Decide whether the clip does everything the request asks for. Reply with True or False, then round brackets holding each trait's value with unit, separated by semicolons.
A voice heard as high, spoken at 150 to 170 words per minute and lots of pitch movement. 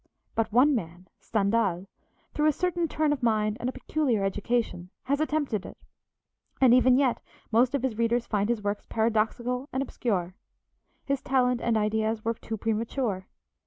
False (230 Hz; 160 wpm; 3.6 semitones)